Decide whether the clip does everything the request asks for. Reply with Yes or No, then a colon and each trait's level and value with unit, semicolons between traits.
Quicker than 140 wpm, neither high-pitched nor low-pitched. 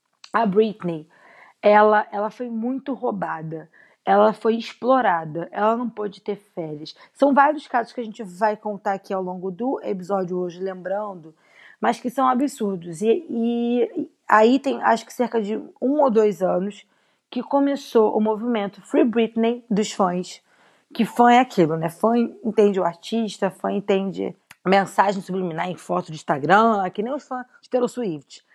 No: average, 165 wpm; high, 215 Hz